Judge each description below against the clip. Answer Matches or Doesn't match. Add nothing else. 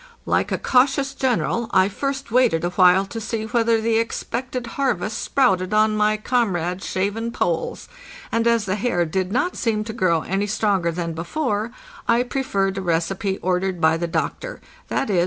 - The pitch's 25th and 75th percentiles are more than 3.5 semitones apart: Matches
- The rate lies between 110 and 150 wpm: Doesn't match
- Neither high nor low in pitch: Doesn't match